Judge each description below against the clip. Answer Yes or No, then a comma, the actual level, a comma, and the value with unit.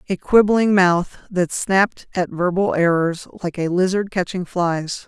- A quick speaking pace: No, average, 155 wpm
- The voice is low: No, medium, 185 Hz